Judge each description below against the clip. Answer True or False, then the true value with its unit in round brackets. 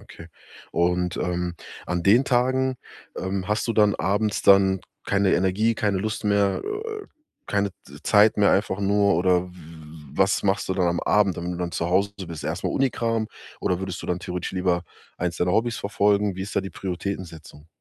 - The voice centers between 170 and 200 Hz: False (95 Hz)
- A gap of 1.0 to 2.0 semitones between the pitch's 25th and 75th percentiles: False (2.7 semitones)